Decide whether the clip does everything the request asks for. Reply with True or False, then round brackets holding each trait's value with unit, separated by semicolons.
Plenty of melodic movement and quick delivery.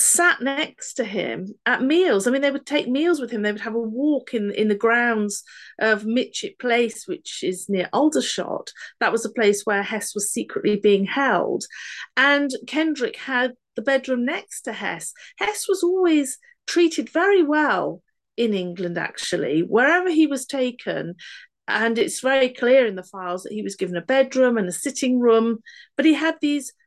False (5.8 semitones; 185 wpm)